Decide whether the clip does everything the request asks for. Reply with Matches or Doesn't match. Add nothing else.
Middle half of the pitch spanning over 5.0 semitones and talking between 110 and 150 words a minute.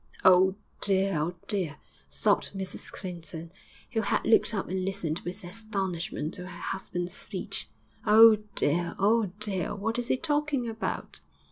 Doesn't match